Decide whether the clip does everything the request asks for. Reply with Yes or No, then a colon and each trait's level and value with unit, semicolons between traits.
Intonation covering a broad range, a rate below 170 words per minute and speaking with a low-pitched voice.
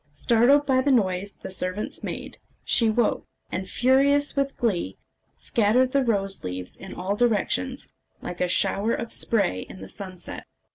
No: wide, 5.7 semitones; average, 155 wpm; high, 215 Hz